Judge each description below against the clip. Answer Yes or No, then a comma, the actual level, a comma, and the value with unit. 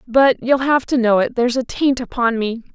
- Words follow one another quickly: Yes, fast, 220 wpm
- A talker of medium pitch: No, high, 245 Hz